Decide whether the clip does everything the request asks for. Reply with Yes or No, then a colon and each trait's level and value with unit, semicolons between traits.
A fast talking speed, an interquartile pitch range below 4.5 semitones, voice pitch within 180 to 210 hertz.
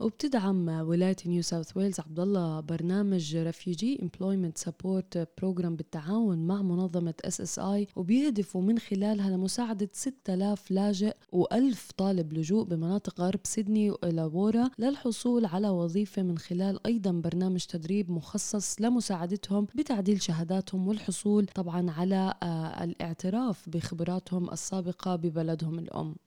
No: average, 115 wpm; average, 3.0 semitones; high, 190 Hz